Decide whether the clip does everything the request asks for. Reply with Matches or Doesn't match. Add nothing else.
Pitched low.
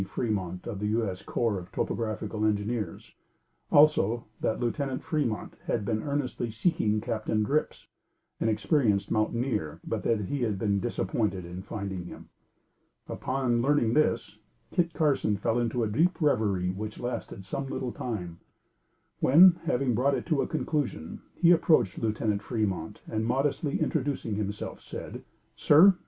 Matches